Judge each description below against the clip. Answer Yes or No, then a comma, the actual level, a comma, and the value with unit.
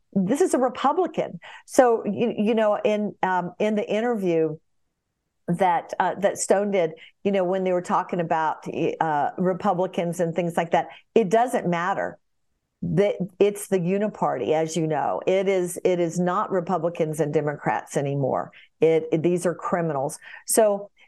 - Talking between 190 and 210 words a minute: No, average, 160 wpm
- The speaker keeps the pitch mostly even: No, average, 4.0 semitones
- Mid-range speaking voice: Yes, medium, 180 Hz